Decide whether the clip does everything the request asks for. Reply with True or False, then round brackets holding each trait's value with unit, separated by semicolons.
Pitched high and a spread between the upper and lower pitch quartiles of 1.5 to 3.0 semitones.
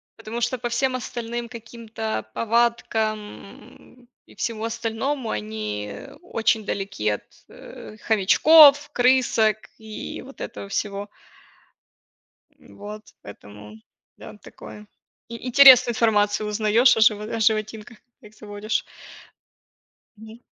True (220 Hz; 2.4 semitones)